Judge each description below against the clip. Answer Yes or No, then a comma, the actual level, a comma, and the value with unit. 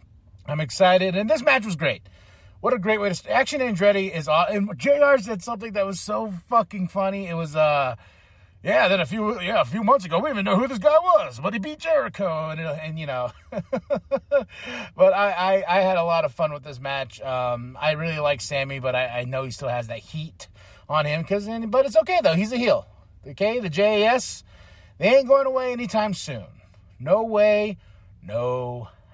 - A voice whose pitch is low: No, medium, 180 Hz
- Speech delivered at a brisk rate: Yes, fast, 210 wpm